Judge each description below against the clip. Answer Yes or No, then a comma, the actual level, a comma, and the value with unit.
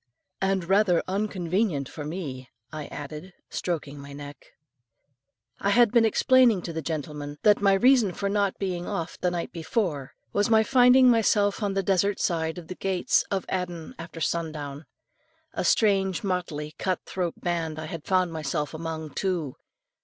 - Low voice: No, medium, 180 Hz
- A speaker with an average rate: Yes, average, 165 wpm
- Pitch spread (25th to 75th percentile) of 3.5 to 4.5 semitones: Yes, average, 4.2 semitones